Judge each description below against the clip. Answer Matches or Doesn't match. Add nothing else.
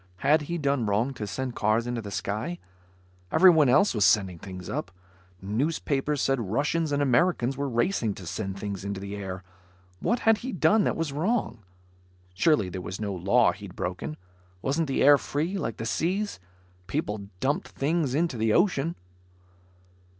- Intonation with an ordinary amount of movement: Doesn't match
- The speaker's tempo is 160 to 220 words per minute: Matches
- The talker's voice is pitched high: Doesn't match